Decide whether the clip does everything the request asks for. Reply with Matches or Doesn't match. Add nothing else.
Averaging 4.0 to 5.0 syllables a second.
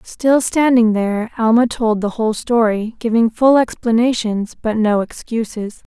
Matches